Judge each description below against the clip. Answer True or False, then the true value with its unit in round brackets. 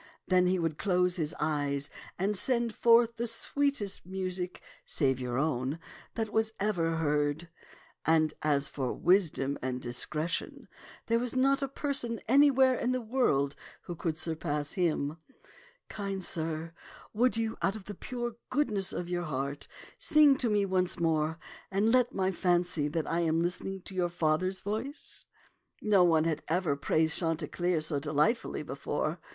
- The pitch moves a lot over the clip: True (6.0 semitones)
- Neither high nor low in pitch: True (180 Hz)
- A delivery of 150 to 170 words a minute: True (160 wpm)